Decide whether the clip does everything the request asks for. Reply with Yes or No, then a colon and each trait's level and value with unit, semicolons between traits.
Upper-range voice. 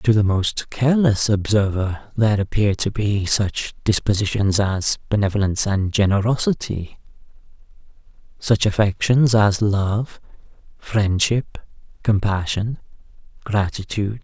No: low, 105 Hz